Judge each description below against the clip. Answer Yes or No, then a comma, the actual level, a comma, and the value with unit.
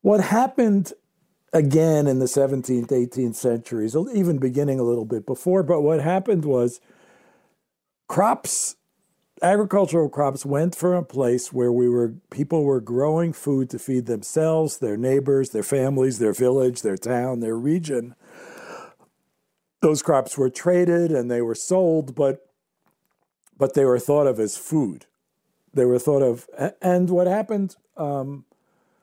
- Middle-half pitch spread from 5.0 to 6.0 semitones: Yes, wide, 5.6 semitones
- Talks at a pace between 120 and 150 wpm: Yes, average, 145 wpm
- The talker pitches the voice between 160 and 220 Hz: No, medium, 140 Hz